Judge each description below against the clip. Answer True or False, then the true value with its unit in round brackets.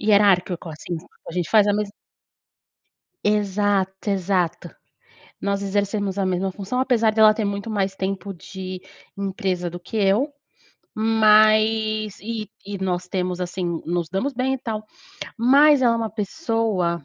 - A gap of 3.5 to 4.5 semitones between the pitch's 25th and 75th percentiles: False (2.6 semitones)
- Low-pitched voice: False (200 Hz)